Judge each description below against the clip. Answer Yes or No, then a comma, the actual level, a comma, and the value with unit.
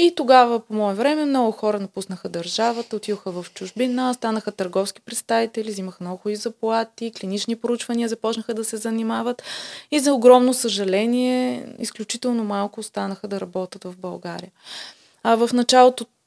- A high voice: Yes, high, 225 Hz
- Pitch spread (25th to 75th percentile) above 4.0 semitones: No, average, 3.0 semitones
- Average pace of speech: Yes, average, 145 wpm